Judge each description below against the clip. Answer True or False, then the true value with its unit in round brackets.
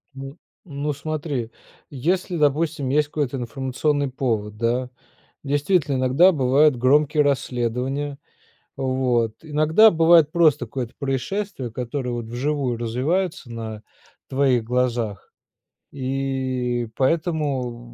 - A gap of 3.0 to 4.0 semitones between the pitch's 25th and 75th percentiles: True (3.4 semitones)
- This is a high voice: False (135 Hz)